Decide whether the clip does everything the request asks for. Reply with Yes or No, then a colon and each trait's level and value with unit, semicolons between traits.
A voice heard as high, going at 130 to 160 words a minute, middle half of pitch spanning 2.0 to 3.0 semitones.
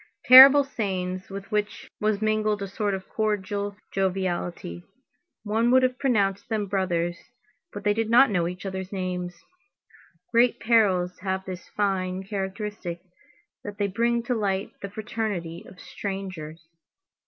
Yes: high, 200 Hz; average, 140 wpm; average, 2.7 semitones